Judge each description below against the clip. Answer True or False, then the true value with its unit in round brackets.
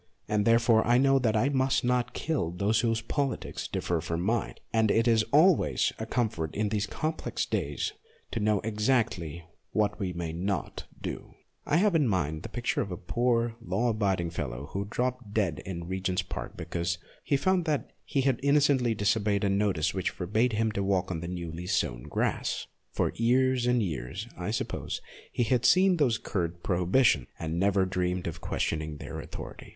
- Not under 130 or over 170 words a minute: False (185 wpm)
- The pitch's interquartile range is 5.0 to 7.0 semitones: True (5.5 semitones)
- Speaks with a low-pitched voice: True (105 Hz)